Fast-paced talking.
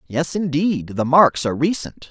No: average, 170 wpm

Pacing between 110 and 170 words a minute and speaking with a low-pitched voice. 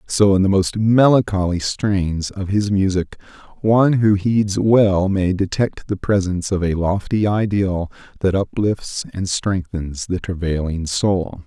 Yes: average, 145 wpm; very low, 95 Hz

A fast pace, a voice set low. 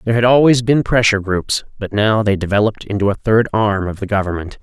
Yes: fast, 220 wpm; low, 105 Hz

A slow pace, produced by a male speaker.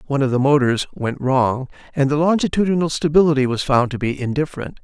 No: average, 185 wpm; male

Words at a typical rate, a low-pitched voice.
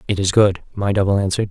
No: fast, 240 wpm; low, 100 Hz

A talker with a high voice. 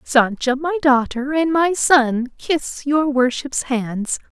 Yes: very high, 275 Hz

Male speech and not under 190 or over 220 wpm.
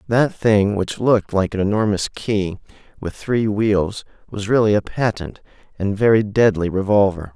No: male; average, 155 wpm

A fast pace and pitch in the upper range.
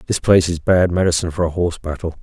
No: fast, 245 wpm; very low, 85 Hz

